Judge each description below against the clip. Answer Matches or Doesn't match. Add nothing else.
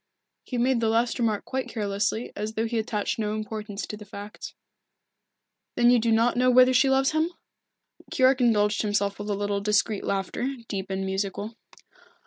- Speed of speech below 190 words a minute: Matches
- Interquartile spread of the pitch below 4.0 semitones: Matches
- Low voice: Doesn't match